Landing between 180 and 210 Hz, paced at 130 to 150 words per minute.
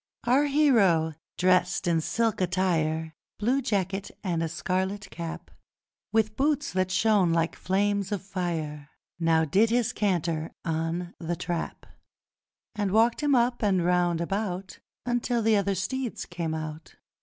Yes: medium, 185 Hz; average, 140 wpm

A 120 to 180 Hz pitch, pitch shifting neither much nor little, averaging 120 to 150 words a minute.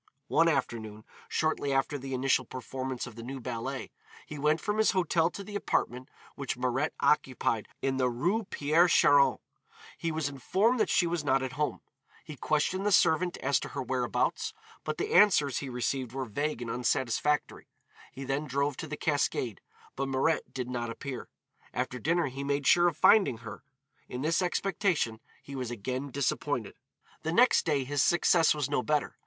No: medium, 140 Hz; average, 4.1 semitones; average, 180 wpm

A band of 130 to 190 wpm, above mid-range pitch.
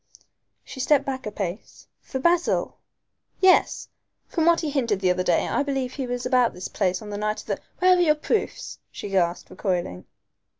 No: average, 200 wpm; very high, 250 Hz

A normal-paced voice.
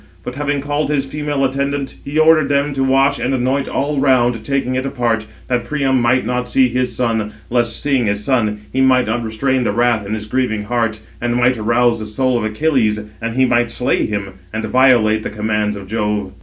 No: fast, 210 wpm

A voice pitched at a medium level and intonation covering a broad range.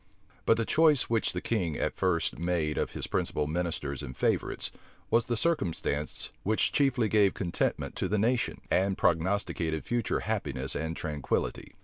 No: very low, 95 Hz; wide, 6.0 semitones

